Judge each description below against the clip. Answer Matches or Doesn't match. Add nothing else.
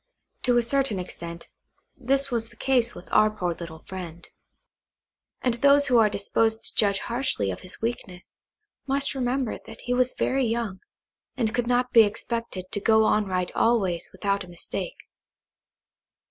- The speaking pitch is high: Matches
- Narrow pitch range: Doesn't match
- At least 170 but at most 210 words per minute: Doesn't match